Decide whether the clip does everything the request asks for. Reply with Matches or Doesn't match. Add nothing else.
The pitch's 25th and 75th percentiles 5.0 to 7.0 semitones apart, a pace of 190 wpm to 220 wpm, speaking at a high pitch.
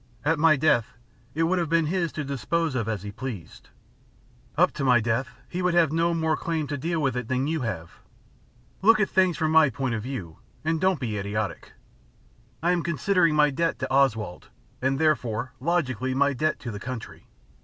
Doesn't match